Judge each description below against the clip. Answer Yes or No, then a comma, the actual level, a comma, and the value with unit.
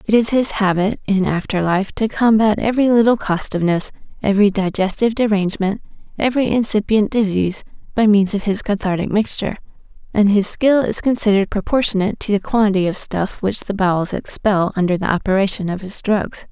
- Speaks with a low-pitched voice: No, high, 205 Hz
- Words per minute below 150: No, average, 165 wpm